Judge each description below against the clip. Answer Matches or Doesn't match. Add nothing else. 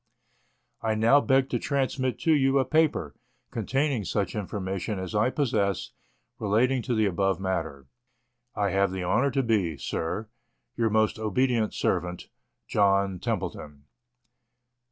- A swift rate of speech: Doesn't match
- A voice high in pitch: Doesn't match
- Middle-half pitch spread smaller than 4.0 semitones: Doesn't match